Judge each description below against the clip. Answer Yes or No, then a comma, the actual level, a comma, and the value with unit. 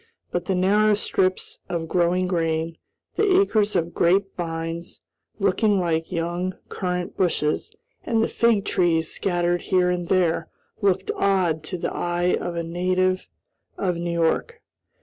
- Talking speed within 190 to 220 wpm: No, average, 145 wpm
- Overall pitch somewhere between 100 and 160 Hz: No, medium, 180 Hz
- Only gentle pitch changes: Yes, narrow, 2.1 semitones